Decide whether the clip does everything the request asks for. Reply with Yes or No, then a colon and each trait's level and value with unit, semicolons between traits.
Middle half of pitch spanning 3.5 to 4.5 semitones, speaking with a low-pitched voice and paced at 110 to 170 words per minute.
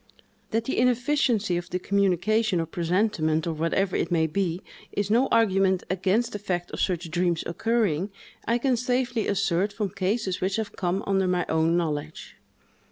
No: average, 4.1 semitones; high, 190 Hz; average, 165 wpm